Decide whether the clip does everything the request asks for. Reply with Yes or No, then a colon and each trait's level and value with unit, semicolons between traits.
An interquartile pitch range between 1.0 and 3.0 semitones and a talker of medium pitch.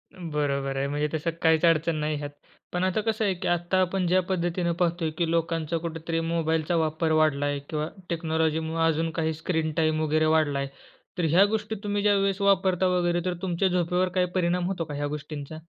Yes: narrow, 2.4 semitones; medium, 165 Hz